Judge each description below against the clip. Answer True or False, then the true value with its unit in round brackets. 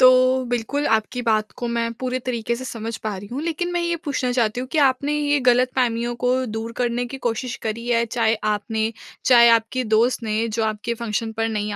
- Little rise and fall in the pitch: True (2.3 semitones)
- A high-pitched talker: True (235 Hz)